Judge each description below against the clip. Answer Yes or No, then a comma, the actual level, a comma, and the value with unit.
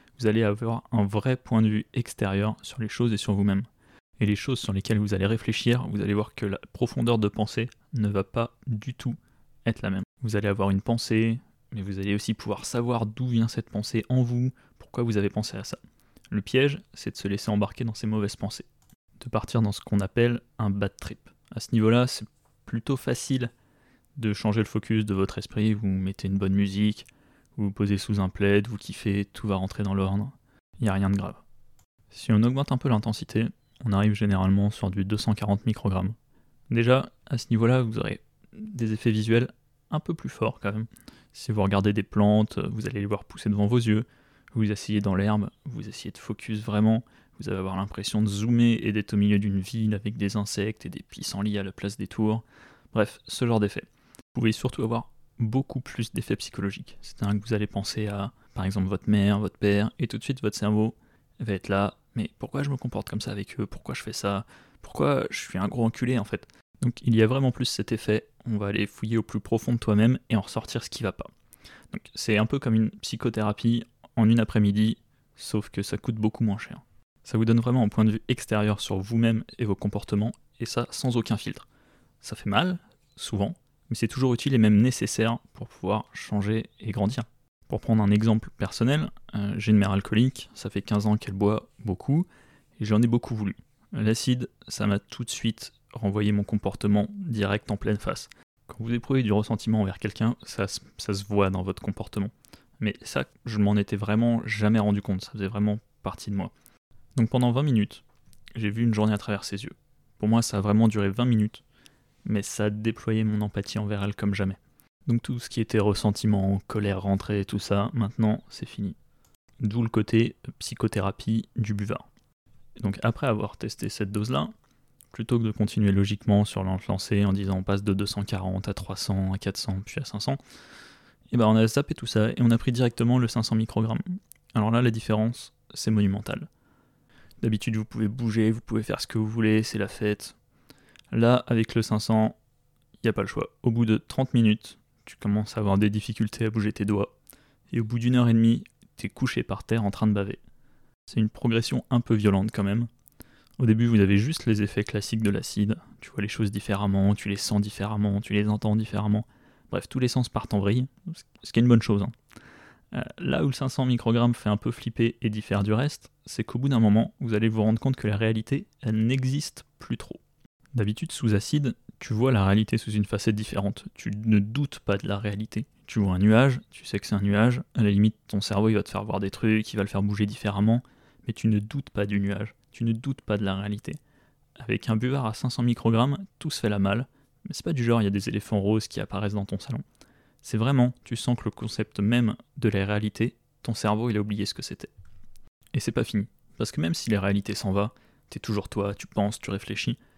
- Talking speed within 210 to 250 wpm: Yes, fast, 220 wpm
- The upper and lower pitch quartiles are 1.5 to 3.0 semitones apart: Yes, narrow, 2.6 semitones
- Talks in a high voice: No, low, 110 Hz